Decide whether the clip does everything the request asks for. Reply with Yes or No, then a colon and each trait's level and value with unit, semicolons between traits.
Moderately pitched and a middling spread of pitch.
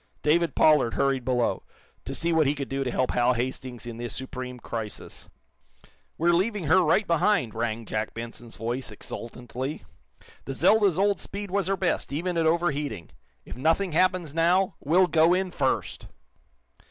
No: medium, 150 Hz; wide, 6.2 semitones